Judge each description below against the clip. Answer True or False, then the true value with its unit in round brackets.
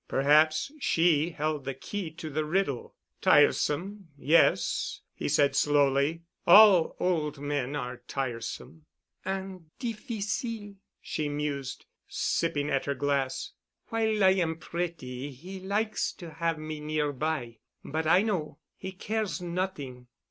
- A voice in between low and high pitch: True (155 Hz)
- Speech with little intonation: False (4.8 semitones)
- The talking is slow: True (125 wpm)